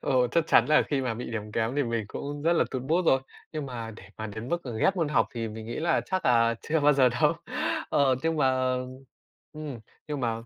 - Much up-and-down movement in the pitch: No, average, 4.6 semitones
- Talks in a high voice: No, low, 130 Hz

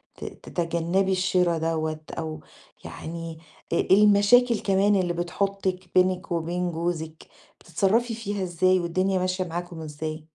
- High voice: No, medium, 180 Hz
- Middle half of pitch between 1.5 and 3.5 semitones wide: Yes, narrow, 2.6 semitones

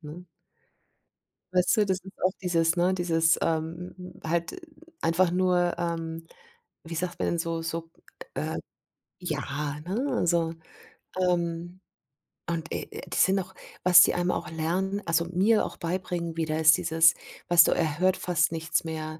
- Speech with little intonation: Yes, narrow, 1.8 semitones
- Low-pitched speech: No, medium, 170 Hz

